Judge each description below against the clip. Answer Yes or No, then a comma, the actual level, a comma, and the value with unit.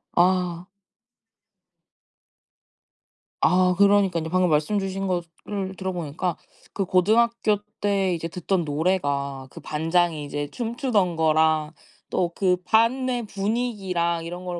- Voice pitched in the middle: Yes, medium, 180 Hz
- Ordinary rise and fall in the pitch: Yes, average, 3.4 semitones